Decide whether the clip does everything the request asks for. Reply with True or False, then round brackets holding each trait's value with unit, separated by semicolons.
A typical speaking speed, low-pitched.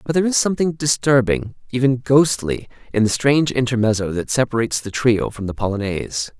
True (170 wpm; 120 Hz)